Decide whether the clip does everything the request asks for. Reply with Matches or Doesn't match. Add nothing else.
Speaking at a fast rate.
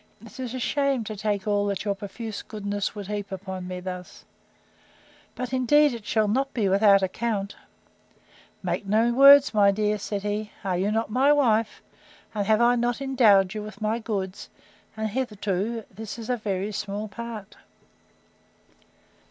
Doesn't match